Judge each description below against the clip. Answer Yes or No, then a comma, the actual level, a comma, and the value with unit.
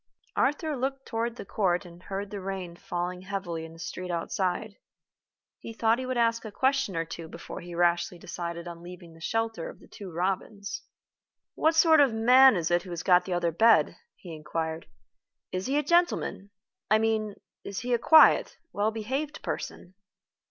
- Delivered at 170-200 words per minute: Yes, average, 185 wpm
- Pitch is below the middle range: No, high, 195 Hz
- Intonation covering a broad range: No, average, 4.9 semitones